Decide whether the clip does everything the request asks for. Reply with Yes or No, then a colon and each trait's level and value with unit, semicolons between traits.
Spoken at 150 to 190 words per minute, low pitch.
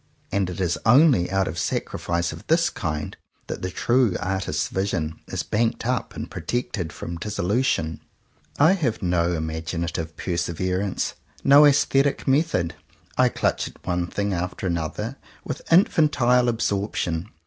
No: slow, 135 wpm; very low, 95 Hz